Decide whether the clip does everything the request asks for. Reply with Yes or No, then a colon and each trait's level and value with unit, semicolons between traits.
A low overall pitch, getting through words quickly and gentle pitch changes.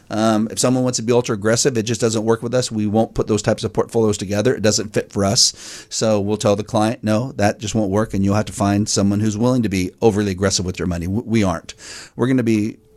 Yes: low, 110 Hz; fast, 270 wpm; narrow, 1.9 semitones